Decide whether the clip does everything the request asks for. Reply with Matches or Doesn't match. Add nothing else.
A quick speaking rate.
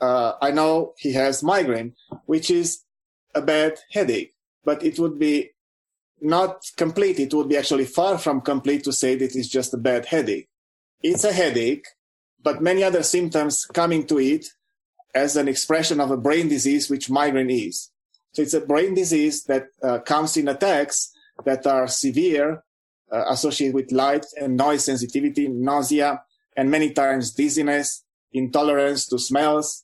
Doesn't match